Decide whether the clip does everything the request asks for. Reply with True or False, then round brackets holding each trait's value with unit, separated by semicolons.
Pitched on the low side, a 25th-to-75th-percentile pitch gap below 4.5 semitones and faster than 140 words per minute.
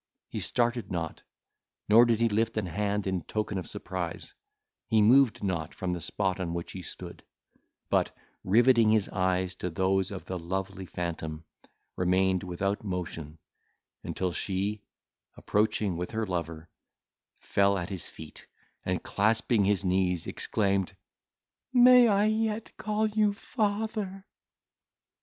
False (100 Hz; 4.1 semitones; 135 wpm)